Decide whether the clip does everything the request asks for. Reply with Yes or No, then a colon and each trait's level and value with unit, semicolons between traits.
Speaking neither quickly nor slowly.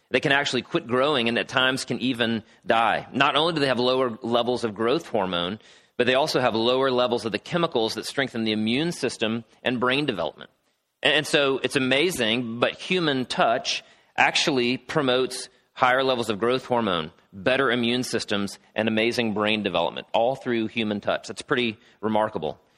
Yes: average, 175 wpm